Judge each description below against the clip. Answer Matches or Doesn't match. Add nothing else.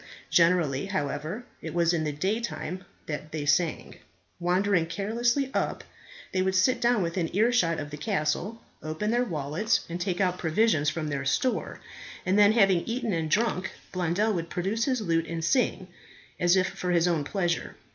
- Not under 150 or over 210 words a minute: Matches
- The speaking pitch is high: Doesn't match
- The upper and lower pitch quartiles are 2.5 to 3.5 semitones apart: Doesn't match